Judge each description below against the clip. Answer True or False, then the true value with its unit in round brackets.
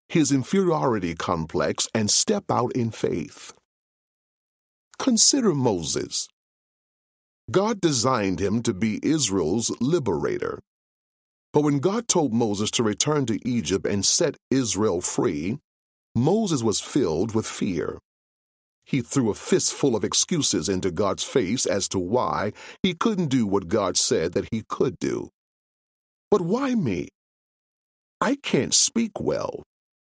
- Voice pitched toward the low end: True (120 Hz)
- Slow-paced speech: True (130 wpm)